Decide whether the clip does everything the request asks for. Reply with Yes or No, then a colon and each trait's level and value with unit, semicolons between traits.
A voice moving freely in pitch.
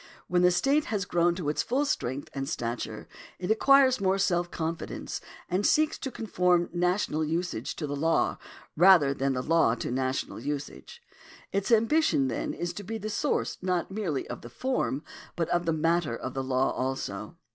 Yes: wide, 6.1 semitones